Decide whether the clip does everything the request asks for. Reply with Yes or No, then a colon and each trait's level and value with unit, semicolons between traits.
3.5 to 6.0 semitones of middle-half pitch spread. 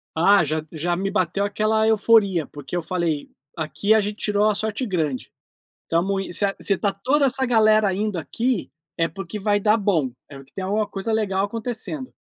Yes: average, 3.8 semitones